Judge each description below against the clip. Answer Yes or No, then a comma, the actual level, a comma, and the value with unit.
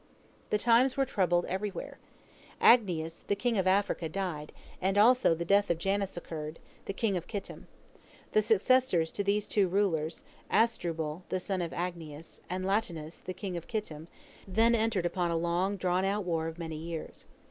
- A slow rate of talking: No, average, 170 wpm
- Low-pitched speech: No, medium, 185 Hz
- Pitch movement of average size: Yes, average, 3.6 semitones